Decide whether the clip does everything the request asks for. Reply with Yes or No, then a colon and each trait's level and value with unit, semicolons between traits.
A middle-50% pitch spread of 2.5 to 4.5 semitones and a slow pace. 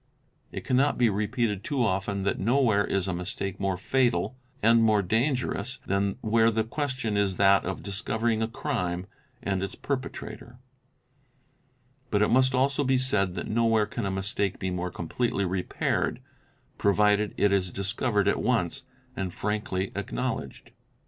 No: average, 3.6 semitones; average, 165 wpm